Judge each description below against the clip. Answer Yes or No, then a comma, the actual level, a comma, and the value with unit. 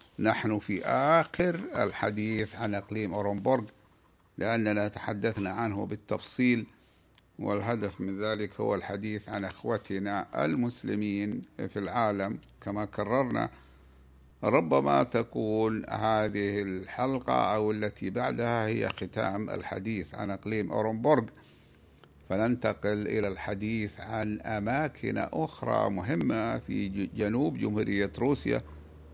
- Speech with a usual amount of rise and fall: No, narrow, 2.0 semitones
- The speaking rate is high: No, average, 95 wpm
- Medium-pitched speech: No, low, 105 Hz